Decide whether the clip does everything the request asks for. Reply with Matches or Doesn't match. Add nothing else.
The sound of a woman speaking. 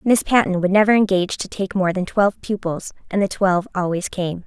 Matches